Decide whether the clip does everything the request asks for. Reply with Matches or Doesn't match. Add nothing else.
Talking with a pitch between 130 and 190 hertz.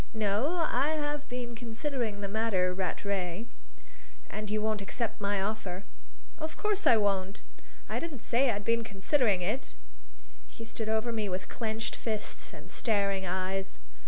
Doesn't match